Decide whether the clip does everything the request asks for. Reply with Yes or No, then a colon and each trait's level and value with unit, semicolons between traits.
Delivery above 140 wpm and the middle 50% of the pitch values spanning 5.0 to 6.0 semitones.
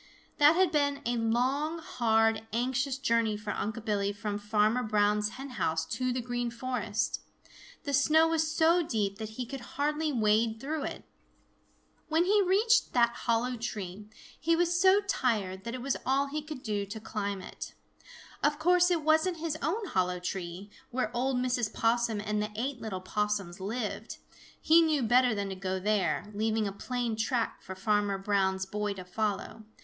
Yes: average, 175 wpm; average, 5.3 semitones